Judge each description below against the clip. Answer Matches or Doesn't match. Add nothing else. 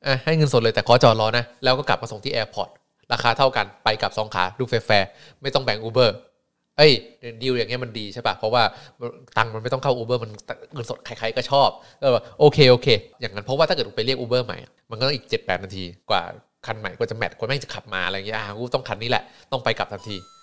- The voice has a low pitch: Matches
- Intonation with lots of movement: Doesn't match